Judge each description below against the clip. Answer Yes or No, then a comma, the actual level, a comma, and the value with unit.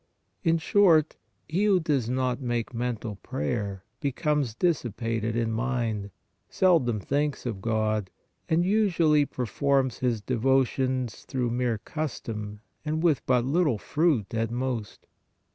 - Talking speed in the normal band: No, slow, 125 wpm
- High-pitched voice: No, low, 125 Hz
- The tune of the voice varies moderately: Yes, average, 4.9 semitones